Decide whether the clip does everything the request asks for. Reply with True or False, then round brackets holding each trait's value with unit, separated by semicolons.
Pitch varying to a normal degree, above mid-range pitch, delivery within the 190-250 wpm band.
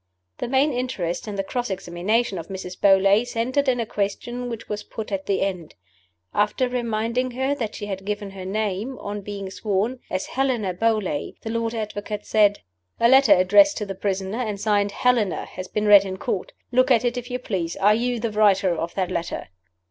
True (3.8 semitones; 210 Hz; 200 wpm)